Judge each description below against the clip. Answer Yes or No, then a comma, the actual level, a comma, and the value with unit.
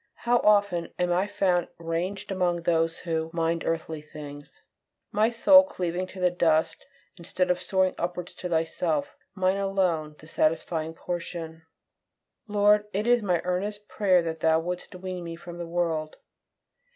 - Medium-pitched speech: Yes, medium, 175 Hz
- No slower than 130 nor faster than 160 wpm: Yes, average, 150 wpm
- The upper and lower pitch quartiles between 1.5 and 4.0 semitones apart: Yes, narrow, 2.4 semitones